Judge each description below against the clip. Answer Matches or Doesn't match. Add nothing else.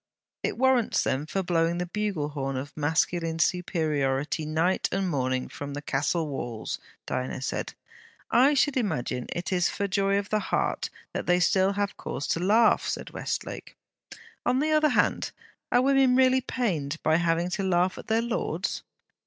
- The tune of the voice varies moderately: Doesn't match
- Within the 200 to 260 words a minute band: Doesn't match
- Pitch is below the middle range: Doesn't match